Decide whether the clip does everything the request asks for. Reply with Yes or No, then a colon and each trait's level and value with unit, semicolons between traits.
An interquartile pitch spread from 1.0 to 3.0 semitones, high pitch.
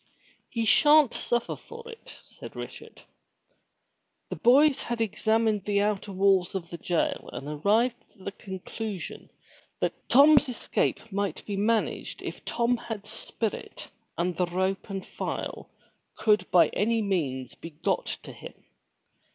No: average, 3.7 semitones; high, 210 Hz